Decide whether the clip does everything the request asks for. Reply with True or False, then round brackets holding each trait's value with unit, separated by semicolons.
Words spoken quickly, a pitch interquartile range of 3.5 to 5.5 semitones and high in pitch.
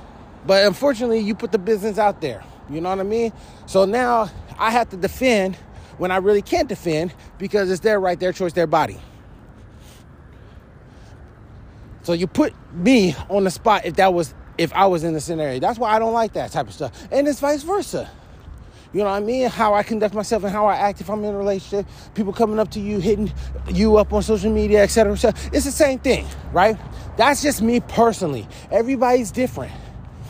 True (210 wpm; 3.9 semitones; 205 Hz)